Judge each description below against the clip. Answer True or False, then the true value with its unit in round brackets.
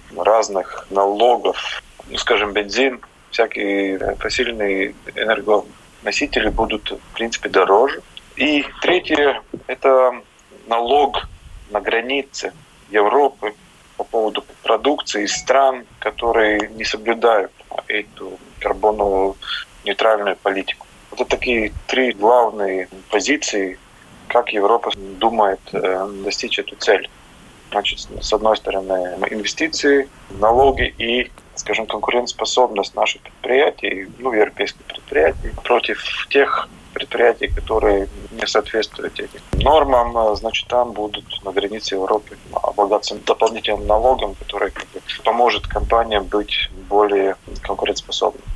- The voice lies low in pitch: True (105 Hz)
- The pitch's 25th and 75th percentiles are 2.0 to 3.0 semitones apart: False (3.5 semitones)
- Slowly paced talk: True (100 wpm)